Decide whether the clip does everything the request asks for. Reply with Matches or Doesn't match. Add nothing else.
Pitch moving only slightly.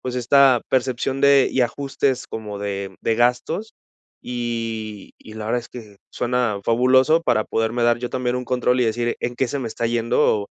Matches